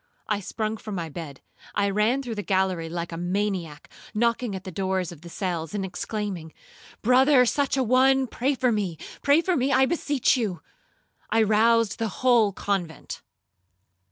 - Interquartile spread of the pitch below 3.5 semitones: No, wide, 5.6 semitones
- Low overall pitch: No, high, 210 Hz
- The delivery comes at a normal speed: Yes, average, 165 wpm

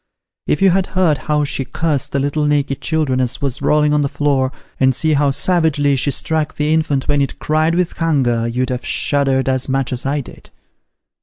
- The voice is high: No, medium, 145 Hz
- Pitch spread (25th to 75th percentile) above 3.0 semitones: No, average, 2.7 semitones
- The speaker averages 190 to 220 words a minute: Yes, fast, 205 wpm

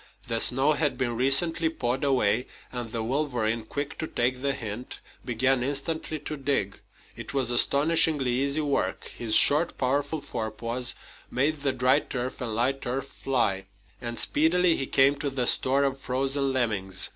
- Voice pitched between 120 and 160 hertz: Yes, low, 135 Hz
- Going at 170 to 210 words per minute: No, average, 160 wpm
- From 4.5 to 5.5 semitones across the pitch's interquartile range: No, average, 2.9 semitones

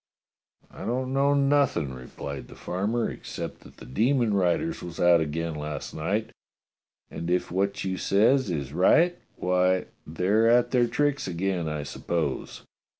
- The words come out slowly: No, average, 150 wpm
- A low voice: Yes, very low, 95 Hz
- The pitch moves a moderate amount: No, wide, 6.6 semitones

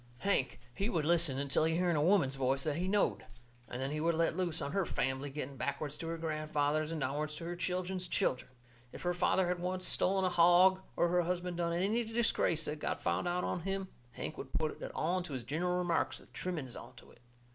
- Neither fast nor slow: No, fast, 225 wpm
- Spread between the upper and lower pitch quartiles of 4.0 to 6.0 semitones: No, average, 3.5 semitones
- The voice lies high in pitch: No, medium, 170 Hz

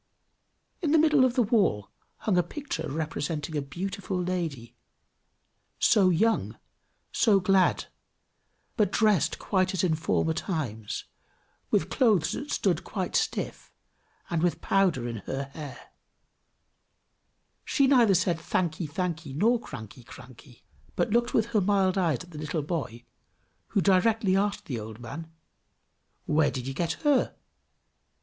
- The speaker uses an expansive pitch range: Yes, wide, 5.7 semitones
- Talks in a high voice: No, medium, 175 Hz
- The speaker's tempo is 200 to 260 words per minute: No, average, 140 wpm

